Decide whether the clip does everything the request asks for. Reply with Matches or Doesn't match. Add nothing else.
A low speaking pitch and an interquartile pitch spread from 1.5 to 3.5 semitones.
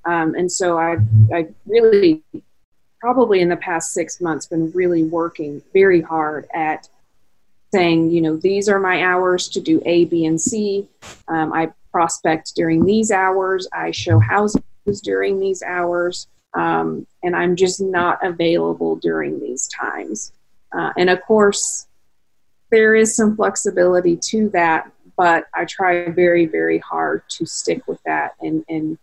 Doesn't match